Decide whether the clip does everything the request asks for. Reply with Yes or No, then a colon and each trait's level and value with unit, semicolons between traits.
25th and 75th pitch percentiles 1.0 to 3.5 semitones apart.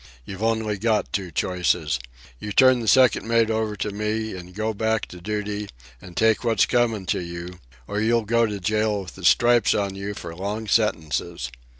Yes: average, 3.1 semitones